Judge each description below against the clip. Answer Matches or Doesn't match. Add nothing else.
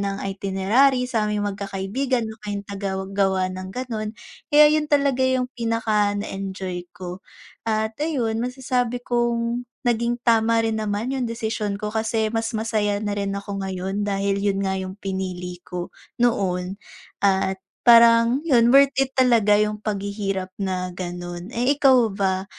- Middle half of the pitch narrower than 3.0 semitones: Doesn't match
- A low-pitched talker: Doesn't match